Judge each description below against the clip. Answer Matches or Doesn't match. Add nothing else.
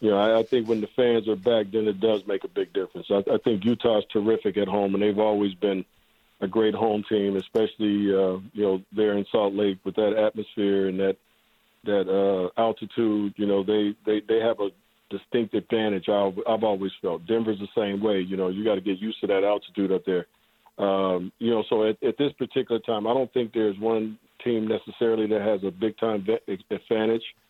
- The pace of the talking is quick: Matches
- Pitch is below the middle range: Matches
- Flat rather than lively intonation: Matches